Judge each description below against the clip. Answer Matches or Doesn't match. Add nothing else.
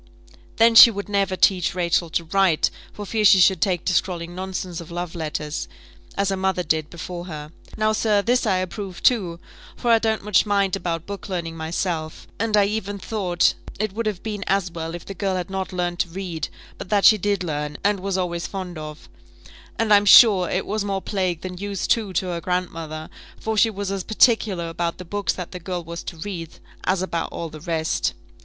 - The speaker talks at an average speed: Doesn't match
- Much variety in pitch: Doesn't match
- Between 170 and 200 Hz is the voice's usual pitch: Matches